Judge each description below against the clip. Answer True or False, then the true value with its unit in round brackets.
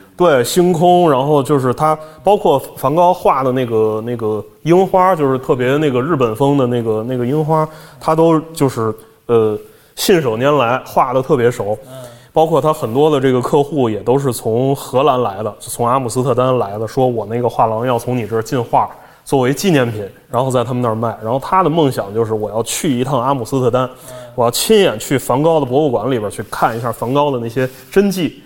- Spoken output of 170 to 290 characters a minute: False (305 characters per minute)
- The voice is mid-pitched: False (130 Hz)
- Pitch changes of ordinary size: True (4.3 semitones)